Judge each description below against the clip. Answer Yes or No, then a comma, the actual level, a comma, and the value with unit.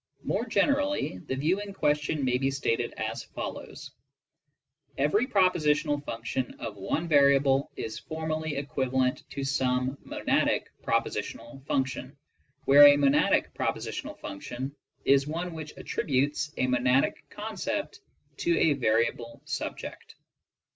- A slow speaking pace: Yes, slow, 120 wpm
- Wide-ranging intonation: No, average, 3.1 semitones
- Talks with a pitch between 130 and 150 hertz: Yes, medium, 140 Hz